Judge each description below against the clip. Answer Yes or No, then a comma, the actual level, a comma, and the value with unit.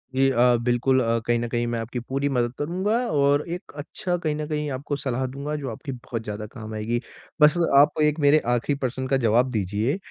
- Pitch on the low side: Yes, low, 130 Hz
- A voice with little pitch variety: No, average, 3.8 semitones